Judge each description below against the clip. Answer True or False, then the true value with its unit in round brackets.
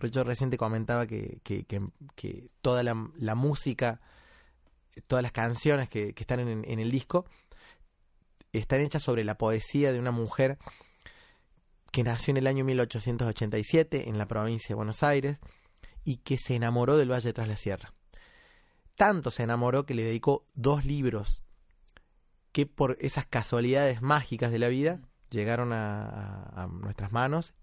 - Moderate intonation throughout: True (3.7 semitones)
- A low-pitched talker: True (120 Hz)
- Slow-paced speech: False (155 wpm)